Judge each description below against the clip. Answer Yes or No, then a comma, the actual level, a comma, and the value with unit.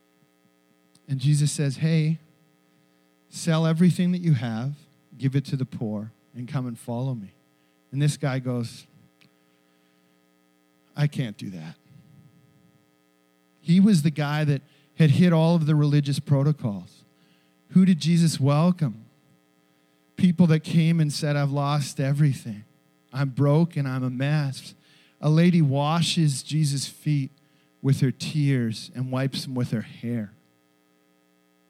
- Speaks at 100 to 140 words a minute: Yes, slow, 135 wpm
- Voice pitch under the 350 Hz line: Yes, low, 135 Hz